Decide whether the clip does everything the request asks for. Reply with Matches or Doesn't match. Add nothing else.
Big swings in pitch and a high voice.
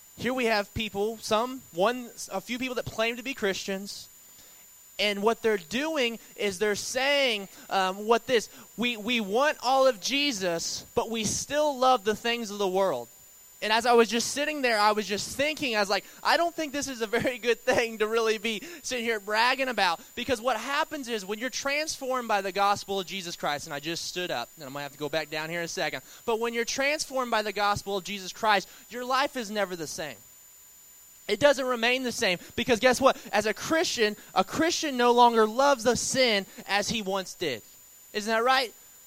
Doesn't match